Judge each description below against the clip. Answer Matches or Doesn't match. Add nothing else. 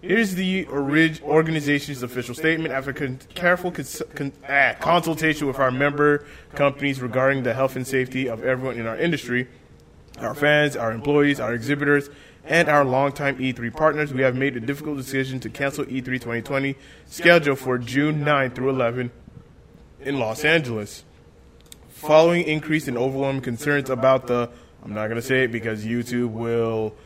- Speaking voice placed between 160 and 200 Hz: Doesn't match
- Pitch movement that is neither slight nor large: Matches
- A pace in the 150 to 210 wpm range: Matches